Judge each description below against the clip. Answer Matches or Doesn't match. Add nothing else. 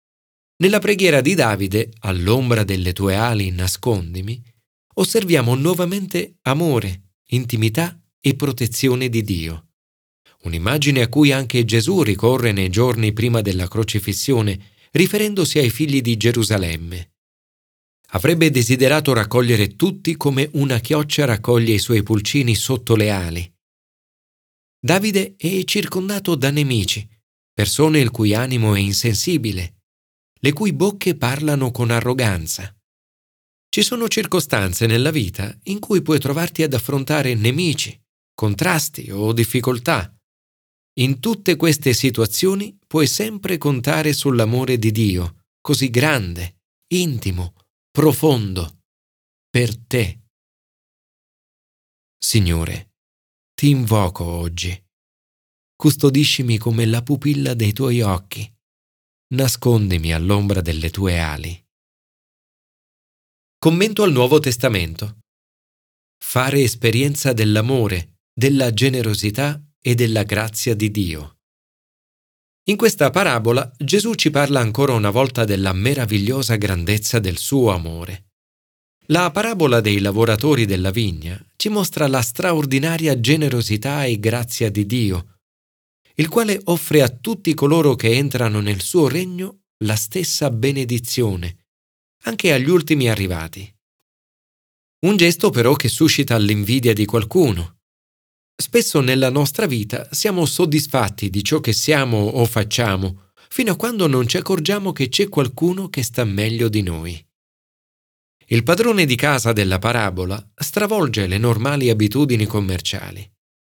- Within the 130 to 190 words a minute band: Doesn't match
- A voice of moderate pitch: Doesn't match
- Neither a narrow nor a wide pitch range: Doesn't match